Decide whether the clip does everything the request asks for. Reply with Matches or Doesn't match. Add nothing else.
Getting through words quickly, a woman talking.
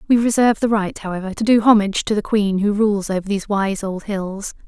Matches